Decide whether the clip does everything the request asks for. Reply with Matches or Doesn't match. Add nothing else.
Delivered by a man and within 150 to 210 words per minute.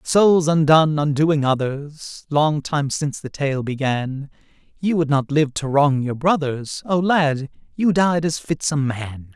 Matches